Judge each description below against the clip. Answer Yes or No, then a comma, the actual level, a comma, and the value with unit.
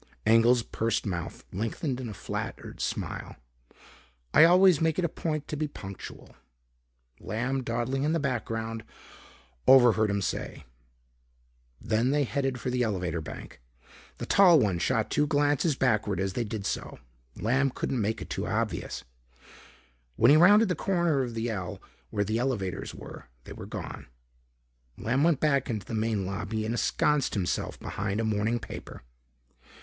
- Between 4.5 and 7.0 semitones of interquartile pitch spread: Yes, average, 5.0 semitones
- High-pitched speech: No, low, 120 Hz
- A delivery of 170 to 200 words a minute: No, average, 155 wpm